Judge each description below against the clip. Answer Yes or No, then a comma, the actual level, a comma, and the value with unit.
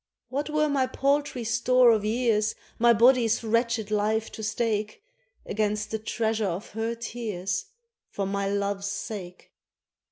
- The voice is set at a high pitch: Yes, high, 220 Hz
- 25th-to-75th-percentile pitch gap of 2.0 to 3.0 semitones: Yes, narrow, 2.4 semitones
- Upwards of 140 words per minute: No, slow, 135 wpm